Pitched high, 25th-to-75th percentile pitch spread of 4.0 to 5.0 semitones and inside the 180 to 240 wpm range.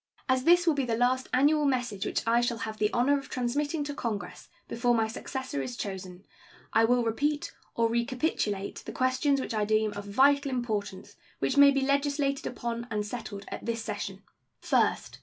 Yes: high, 240 Hz; average, 4.3 semitones; average, 185 wpm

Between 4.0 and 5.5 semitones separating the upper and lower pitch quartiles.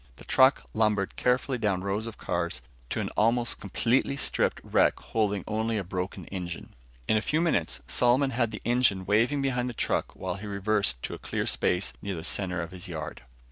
Yes: average, 4.6 semitones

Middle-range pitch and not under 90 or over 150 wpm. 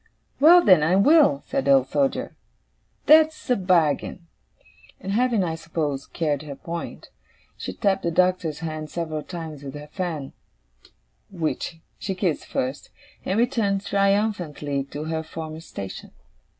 Yes: medium, 170 Hz; average, 140 wpm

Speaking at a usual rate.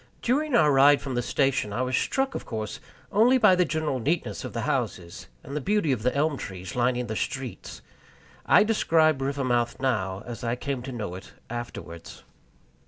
Yes: average, 185 wpm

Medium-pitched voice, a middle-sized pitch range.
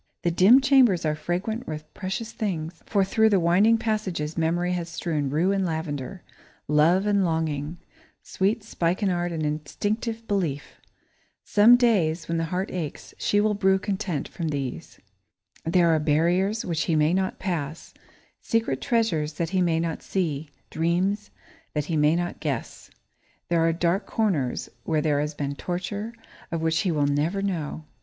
Yes: medium, 175 Hz; average, 4.1 semitones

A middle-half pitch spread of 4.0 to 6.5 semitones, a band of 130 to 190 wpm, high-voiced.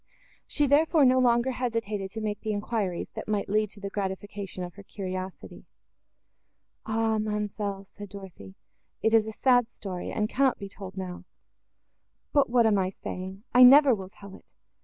No: average, 3.3 semitones; average, 170 wpm; high, 210 Hz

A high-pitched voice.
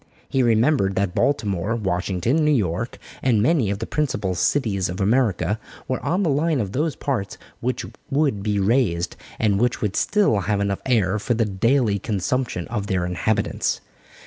No: low, 110 Hz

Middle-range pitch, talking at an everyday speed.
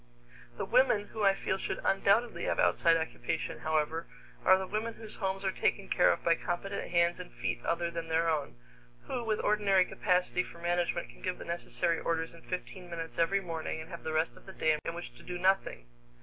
No: medium, 175 Hz; fast, 210 wpm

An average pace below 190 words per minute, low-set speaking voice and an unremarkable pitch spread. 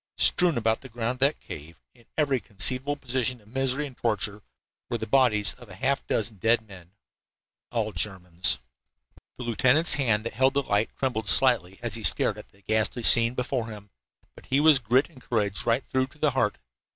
No: average, 195 wpm; low, 120 Hz; average, 3.8 semitones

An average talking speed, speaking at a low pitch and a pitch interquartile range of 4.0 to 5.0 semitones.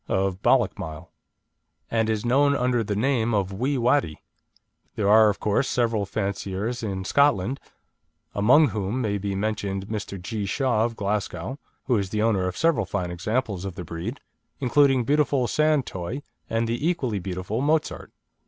Yes: average, 160 wpm; low, 110 Hz; average, 4.7 semitones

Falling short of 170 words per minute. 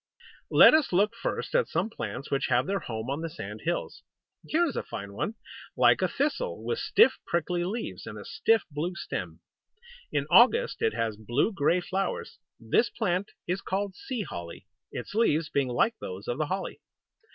No: average, 185 wpm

